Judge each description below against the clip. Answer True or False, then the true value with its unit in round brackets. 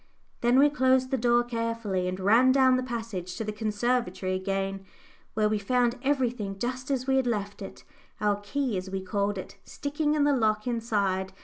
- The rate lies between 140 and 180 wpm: False (190 wpm)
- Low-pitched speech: False (230 Hz)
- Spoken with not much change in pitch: False (4.3 semitones)